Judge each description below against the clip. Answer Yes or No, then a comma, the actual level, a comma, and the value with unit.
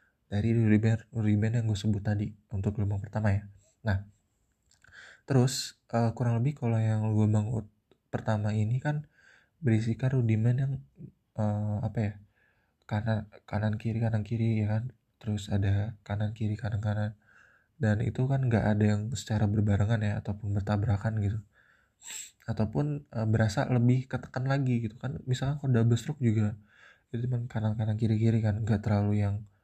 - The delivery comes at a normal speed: No, fast, 145 wpm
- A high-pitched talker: No, low, 110 Hz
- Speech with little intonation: Yes, narrow, 2.0 semitones